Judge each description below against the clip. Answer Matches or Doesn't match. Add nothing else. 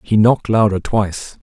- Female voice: Doesn't match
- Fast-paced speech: Doesn't match